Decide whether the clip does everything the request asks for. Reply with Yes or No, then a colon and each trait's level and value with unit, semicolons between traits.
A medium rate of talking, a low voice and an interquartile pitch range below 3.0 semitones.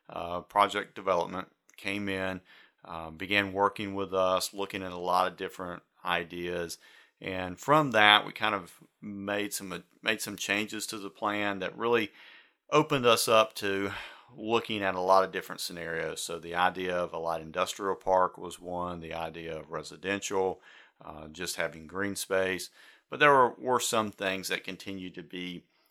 Yes: average, 170 wpm; very low, 95 Hz; narrow, 2.4 semitones